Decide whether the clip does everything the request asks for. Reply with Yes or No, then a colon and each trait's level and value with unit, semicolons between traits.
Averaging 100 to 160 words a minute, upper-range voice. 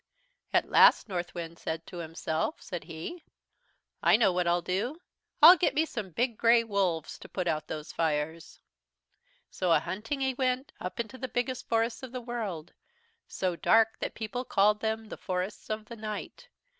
No: average, 170 wpm; high, 210 Hz